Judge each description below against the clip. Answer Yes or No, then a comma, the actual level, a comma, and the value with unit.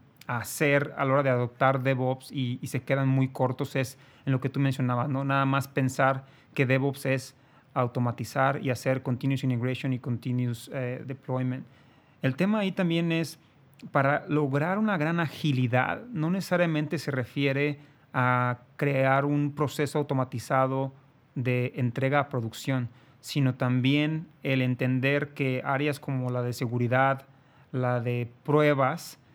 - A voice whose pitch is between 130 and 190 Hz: Yes, low, 135 Hz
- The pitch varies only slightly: Yes, narrow, 2.0 semitones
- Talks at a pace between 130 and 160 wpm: Yes, average, 145 wpm